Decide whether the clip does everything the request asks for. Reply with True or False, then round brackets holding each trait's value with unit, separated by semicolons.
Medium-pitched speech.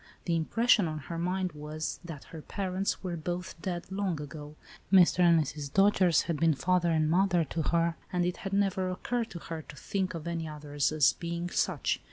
True (170 Hz)